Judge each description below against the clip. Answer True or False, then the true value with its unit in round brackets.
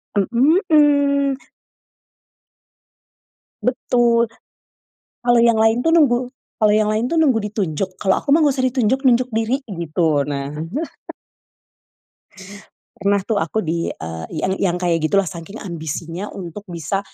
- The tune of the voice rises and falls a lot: True (6.6 semitones)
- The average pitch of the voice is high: True (215 Hz)